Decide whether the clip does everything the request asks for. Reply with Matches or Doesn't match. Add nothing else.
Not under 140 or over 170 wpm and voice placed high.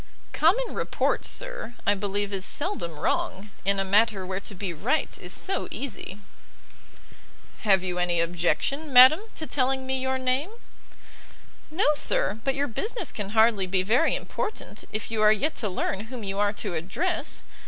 Matches